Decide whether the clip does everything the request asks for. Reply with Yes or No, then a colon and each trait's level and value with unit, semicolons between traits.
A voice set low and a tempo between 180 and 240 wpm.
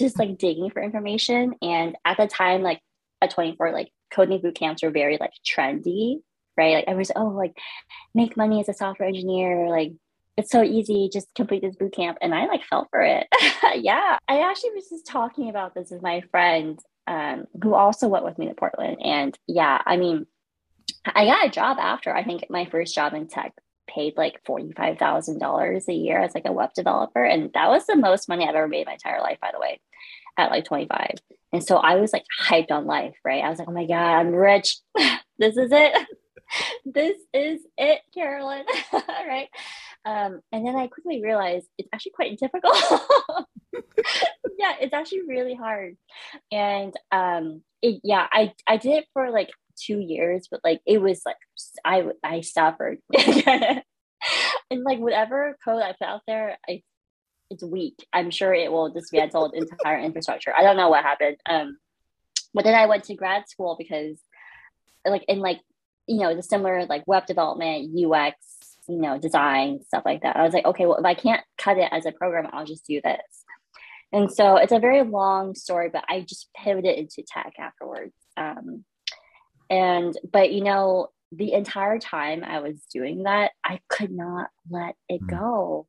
No: high, 190 Hz; average, 190 wpm